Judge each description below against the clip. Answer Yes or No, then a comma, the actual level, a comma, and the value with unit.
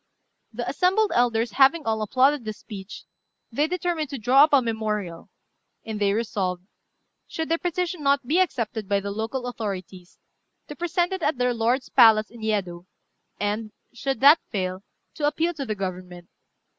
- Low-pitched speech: No, high, 230 Hz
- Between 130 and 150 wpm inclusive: No, average, 165 wpm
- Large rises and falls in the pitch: Yes, wide, 6.2 semitones